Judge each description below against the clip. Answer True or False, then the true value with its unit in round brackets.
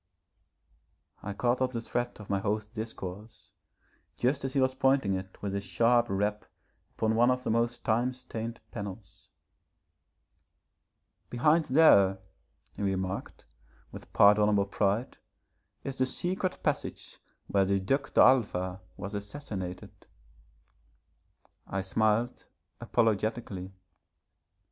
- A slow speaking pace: True (115 wpm)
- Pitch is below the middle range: True (110 Hz)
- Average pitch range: True (4.0 semitones)